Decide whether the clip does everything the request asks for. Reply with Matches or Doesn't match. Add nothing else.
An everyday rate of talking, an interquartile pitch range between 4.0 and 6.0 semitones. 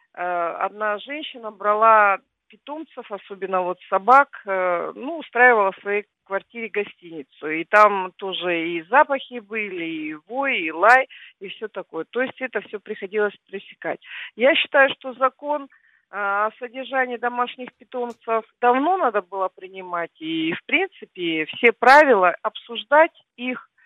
Matches